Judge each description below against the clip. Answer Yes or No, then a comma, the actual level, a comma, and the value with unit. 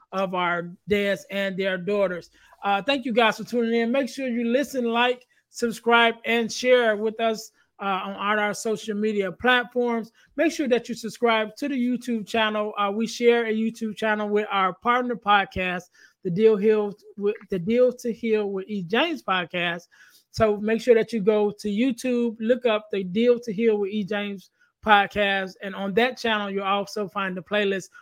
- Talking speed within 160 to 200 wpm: Yes, average, 190 wpm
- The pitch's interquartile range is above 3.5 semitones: No, average, 2.9 semitones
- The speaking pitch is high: Yes, high, 215 Hz